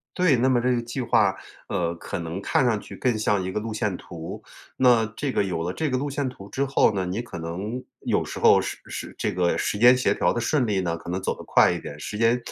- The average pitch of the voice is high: No, low, 110 Hz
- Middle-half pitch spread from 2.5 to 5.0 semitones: No, wide, 5.6 semitones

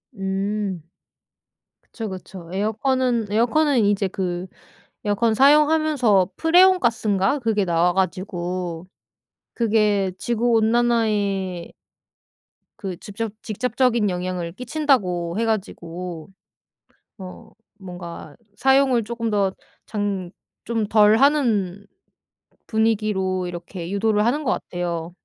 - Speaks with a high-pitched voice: Yes, high, 205 Hz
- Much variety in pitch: No, average, 4.1 semitones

